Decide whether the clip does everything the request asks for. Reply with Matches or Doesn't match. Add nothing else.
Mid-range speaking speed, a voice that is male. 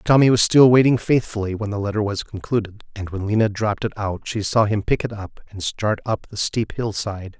Doesn't match